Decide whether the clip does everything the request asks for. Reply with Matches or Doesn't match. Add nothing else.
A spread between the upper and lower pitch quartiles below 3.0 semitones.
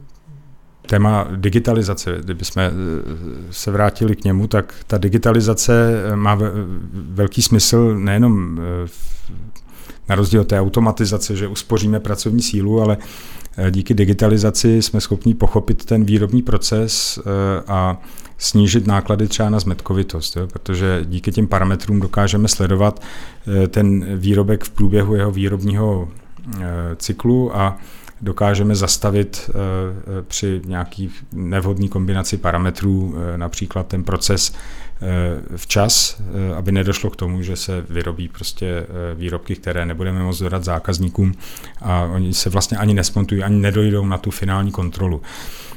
Matches